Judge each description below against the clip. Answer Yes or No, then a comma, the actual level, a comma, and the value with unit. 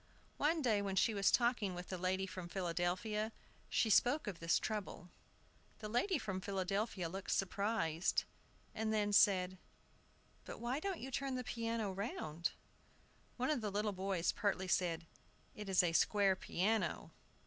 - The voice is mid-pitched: No, high, 200 Hz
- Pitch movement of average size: Yes, average, 3.4 semitones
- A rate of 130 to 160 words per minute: Yes, average, 155 wpm